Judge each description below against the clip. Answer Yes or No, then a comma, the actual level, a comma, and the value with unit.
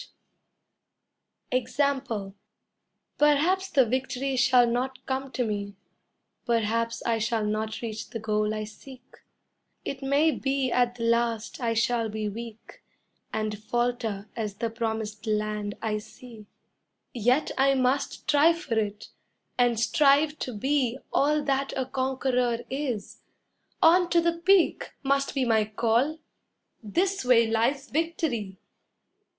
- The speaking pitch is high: Yes, high, 245 Hz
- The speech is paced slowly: Yes, slow, 130 wpm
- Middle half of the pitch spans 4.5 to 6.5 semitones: No, average, 3.8 semitones